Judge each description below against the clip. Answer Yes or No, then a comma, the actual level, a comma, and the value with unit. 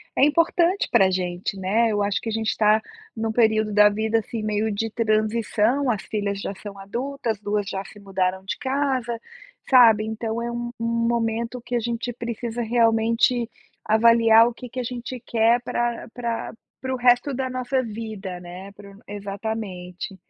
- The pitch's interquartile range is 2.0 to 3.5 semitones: Yes, narrow, 2.5 semitones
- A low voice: No, high, 225 Hz